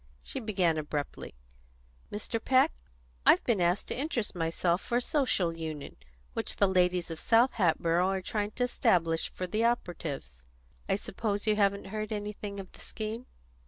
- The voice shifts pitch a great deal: No, average, 4.3 semitones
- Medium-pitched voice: No, high, 195 Hz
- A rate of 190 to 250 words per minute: No, average, 160 wpm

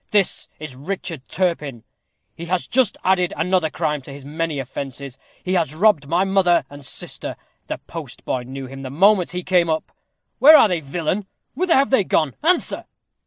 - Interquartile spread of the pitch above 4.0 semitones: Yes, average, 5.2 semitones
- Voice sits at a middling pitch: Yes, medium, 165 Hz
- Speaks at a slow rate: No, average, 175 wpm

